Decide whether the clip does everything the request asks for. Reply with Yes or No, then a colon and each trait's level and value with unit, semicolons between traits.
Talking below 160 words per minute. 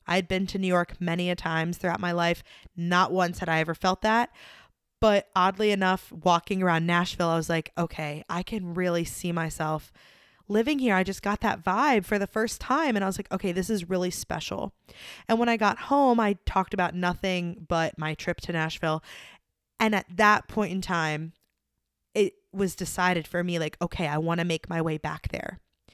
No: average, 200 wpm